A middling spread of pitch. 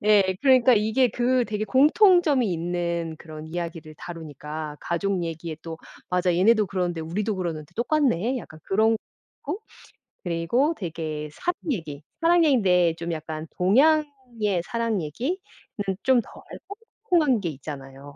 No: wide, 7.0 semitones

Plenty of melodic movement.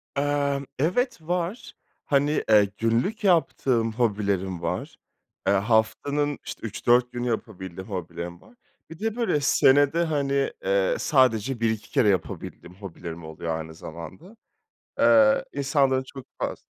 Yes: wide, 6.9 semitones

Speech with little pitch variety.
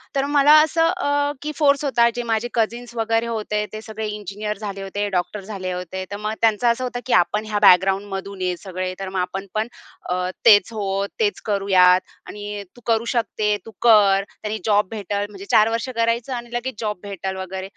No: average, 3.2 semitones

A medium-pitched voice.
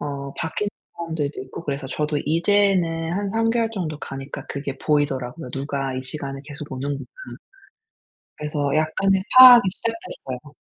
Yes: medium, 150 Hz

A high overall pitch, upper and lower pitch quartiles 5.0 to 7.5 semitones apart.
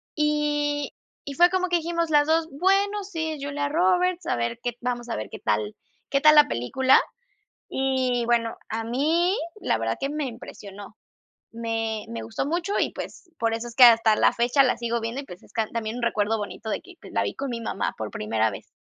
Yes: very high, 250 Hz; average, 5.3 semitones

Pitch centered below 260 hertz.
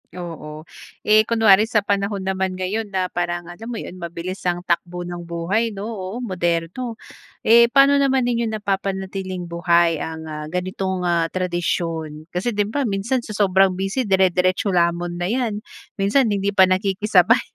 Yes: high, 190 Hz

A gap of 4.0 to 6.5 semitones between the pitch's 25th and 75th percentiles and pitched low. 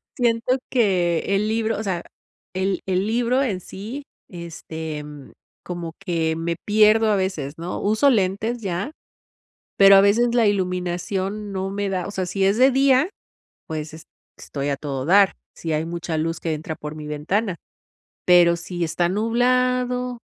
No: average, 4.6 semitones; high, 190 Hz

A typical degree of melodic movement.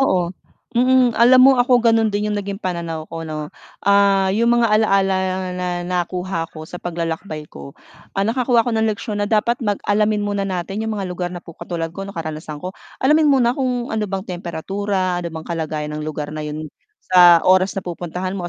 Yes: average, 4.0 semitones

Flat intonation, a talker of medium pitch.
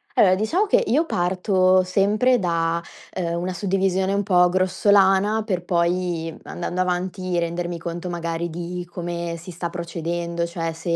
Yes: narrow, 1.8 semitones; medium, 180 Hz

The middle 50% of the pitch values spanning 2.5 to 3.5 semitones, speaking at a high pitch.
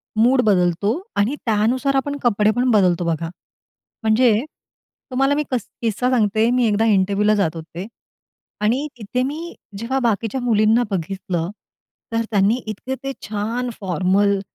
No: average, 4.0 semitones; high, 215 Hz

